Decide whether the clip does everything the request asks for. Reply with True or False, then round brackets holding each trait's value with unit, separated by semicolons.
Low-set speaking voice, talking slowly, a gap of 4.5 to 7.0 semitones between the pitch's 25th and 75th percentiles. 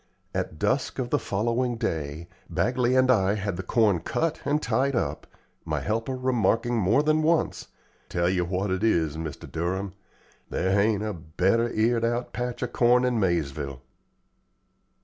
False (110 Hz; 160 wpm; 5.3 semitones)